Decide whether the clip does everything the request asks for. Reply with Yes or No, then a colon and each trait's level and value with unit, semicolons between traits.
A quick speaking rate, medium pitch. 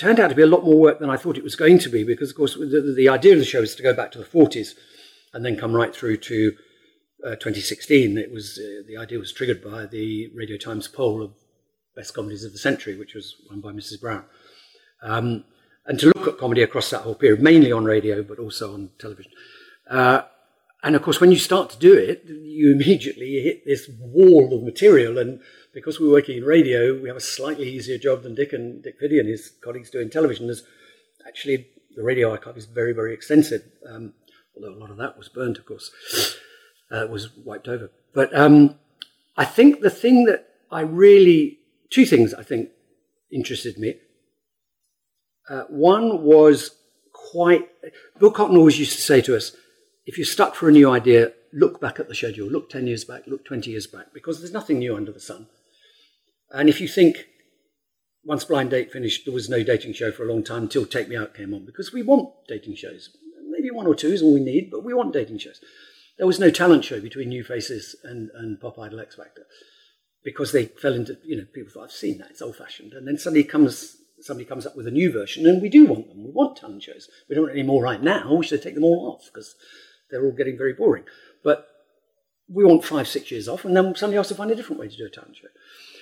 Yes: fast, 225 wpm; medium, 155 Hz